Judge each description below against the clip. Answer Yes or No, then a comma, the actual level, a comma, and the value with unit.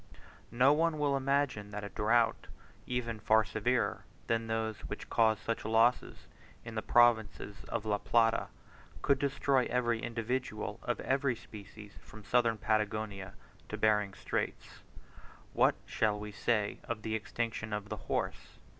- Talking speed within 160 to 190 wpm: No, average, 145 wpm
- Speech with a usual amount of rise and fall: No, narrow, 2.3 semitones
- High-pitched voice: No, low, 110 Hz